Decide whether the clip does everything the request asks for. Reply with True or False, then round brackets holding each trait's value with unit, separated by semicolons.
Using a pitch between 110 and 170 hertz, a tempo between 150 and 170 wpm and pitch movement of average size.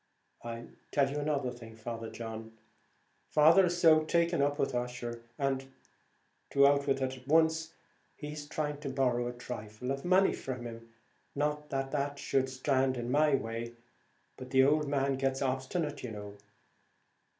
True (135 Hz; 160 wpm; 3.3 semitones)